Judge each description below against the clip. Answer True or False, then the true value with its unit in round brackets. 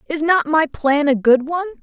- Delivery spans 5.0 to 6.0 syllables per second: True (5.4 syllables/s)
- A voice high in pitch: True (305 Hz)